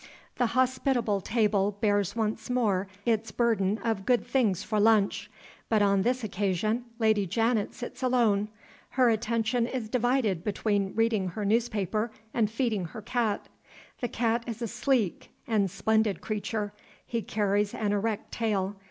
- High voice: Yes, high, 220 Hz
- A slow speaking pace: No, average, 145 wpm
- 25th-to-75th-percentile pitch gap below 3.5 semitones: Yes, narrow, 2.5 semitones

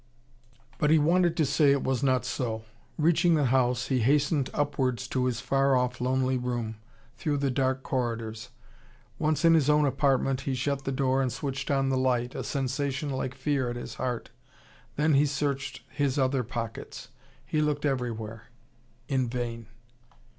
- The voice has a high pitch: No, low, 135 Hz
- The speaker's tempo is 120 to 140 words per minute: No, average, 170 wpm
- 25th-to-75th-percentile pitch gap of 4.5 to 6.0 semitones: No, narrow, 2.4 semitones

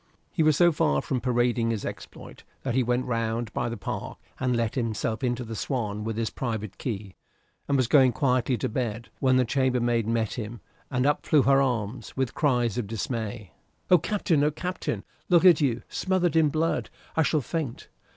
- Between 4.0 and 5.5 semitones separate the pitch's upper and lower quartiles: No, average, 3.6 semitones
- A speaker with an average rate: Yes, average, 190 wpm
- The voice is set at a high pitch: No, low, 125 Hz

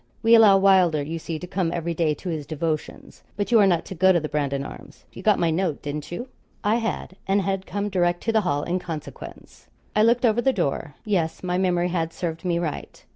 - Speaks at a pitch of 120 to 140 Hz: No, medium, 180 Hz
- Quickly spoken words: Yes, fast, 235 wpm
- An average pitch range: Yes, average, 3.5 semitones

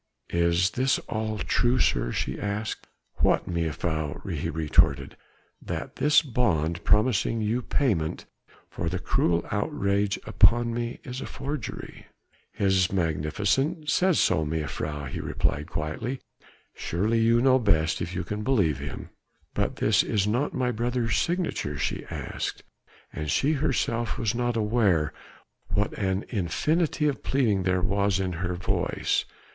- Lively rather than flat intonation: Yes, wide, 6.3 semitones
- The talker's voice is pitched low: Yes, low, 100 Hz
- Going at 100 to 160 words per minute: Yes, average, 140 wpm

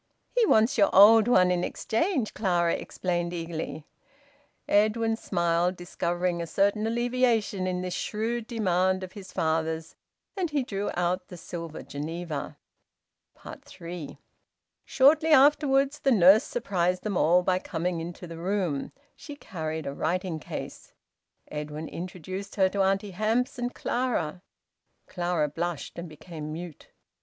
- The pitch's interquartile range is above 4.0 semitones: Yes, average, 4.5 semitones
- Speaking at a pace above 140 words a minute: No, slow, 135 wpm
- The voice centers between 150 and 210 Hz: Yes, medium, 185 Hz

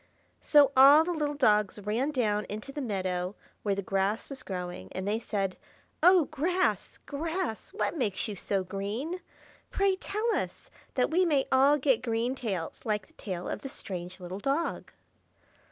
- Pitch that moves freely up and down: Yes, wide, 6.9 semitones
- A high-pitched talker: Yes, high, 235 Hz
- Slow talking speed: No, average, 170 wpm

